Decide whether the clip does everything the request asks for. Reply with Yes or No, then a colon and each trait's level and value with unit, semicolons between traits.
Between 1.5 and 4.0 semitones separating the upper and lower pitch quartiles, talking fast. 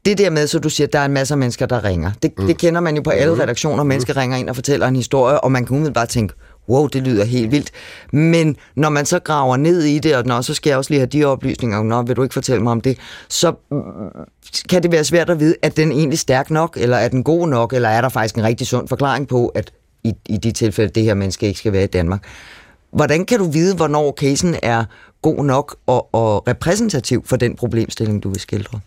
No: average, 4.6 semitones; fast, 260 wpm